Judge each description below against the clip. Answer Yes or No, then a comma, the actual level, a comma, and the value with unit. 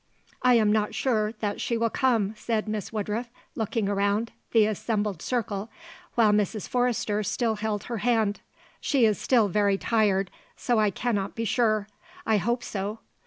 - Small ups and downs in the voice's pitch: Yes, narrow, 2.1 semitones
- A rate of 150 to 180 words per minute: Yes, average, 165 wpm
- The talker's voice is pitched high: Yes, high, 215 Hz